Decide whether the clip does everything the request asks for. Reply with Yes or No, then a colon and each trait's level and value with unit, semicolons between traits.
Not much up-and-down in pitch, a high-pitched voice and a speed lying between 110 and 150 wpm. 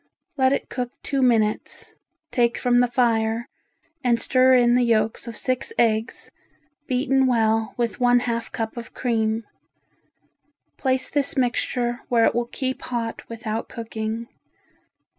Yes: narrow, 1.9 semitones; high, 240 Hz; average, 140 wpm